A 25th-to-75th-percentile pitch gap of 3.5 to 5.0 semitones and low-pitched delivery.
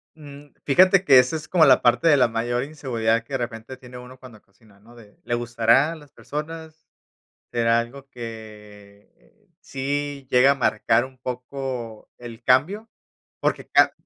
Yes: average, 3.8 semitones; low, 125 Hz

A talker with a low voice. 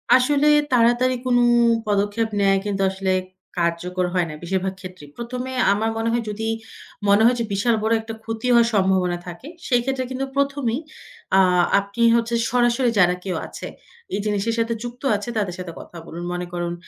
No: high, 220 Hz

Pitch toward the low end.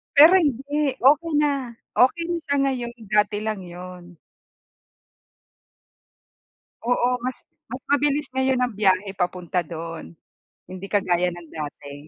No: high, 225 Hz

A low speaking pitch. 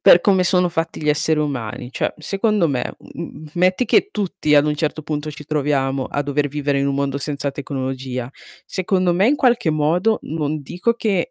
No: medium, 150 Hz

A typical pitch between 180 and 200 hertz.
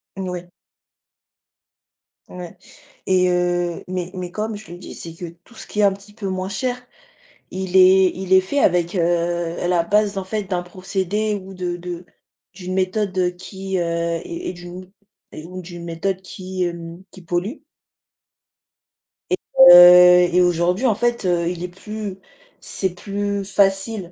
Yes: medium, 185 Hz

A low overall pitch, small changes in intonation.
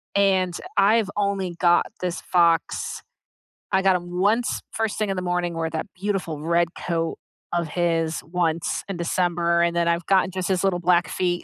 No: medium, 175 Hz; narrow, 2.0 semitones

